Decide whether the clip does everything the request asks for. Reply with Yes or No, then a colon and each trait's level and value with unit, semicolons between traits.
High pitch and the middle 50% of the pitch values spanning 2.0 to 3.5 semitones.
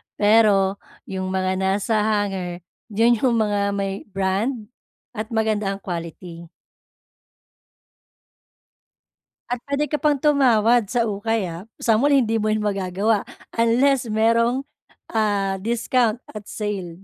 Yes: high, 215 Hz; average, 3.0 semitones